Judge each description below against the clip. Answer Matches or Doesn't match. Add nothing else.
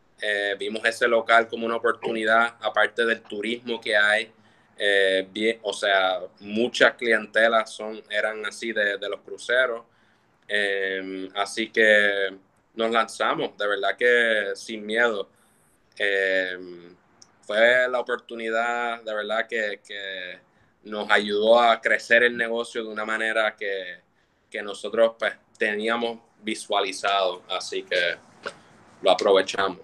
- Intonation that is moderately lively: Doesn't match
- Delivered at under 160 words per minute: Matches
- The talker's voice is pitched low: Matches